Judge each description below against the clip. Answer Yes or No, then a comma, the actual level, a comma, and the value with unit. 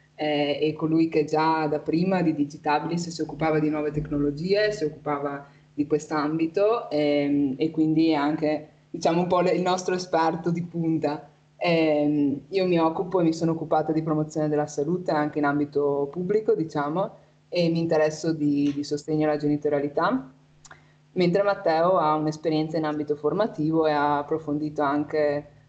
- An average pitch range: No, narrow, 1.7 semitones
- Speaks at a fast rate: No, average, 160 wpm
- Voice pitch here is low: No, medium, 155 Hz